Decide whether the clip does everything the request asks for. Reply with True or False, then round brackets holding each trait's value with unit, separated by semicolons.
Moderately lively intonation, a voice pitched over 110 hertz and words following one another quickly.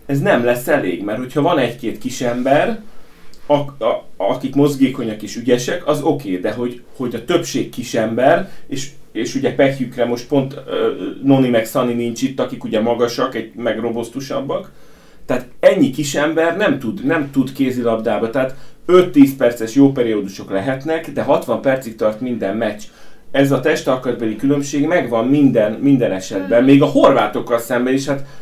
True (3.3 semitones; 130 Hz; 165 wpm)